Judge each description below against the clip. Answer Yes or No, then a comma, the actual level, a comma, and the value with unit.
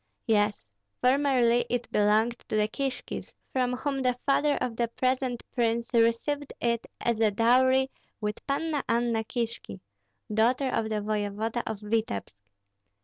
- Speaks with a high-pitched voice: Yes, high, 235 Hz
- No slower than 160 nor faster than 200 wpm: No, slow, 135 wpm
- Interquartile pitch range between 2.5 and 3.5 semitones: Yes, average, 2.8 semitones